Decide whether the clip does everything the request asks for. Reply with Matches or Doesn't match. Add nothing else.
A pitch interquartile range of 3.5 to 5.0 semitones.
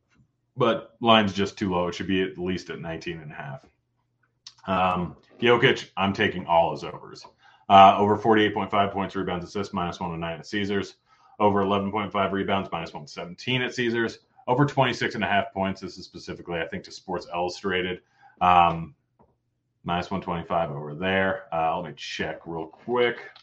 Matches